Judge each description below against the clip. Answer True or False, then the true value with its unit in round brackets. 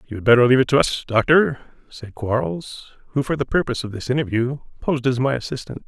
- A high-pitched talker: False (125 Hz)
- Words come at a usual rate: False (215 wpm)